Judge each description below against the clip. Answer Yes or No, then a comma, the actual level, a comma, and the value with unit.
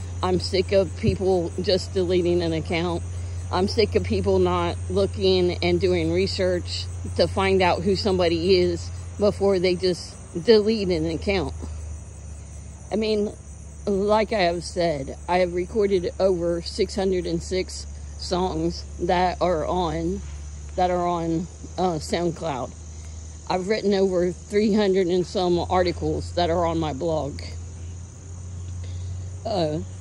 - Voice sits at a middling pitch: No, low, 100 Hz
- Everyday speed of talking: No, slow, 130 wpm